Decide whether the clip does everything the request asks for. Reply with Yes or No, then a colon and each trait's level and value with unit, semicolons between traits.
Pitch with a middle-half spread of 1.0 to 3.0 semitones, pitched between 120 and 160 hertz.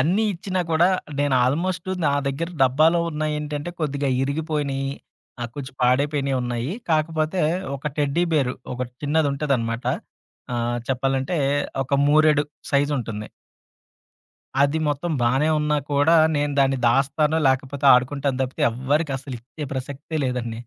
Yes: average, 2.7 semitones; medium, 140 Hz